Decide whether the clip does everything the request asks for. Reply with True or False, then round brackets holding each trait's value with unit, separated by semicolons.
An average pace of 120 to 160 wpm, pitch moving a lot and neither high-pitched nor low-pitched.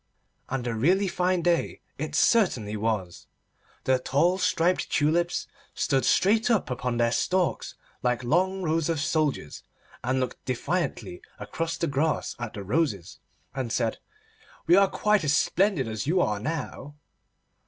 True (145 wpm; 6.6 semitones; 150 Hz)